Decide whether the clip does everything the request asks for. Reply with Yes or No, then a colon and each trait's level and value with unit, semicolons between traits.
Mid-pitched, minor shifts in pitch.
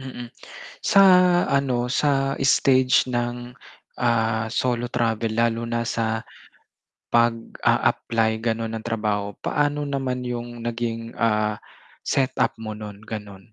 No: low, 115 Hz; narrow, 1.9 semitones